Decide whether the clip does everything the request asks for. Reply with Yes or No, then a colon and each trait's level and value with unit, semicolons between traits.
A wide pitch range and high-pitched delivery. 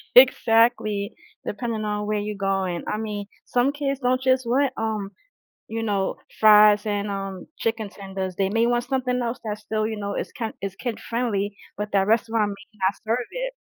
No: average, 2.9 semitones; high, 215 Hz